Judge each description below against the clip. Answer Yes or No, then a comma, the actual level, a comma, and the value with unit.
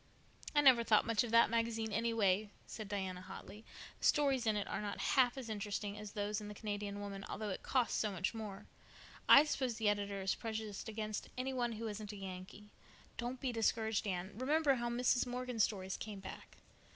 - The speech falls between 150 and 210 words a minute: Yes, average, 200 wpm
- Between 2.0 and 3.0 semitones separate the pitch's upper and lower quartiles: Yes, average, 2.7 semitones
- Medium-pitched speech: No, high, 215 Hz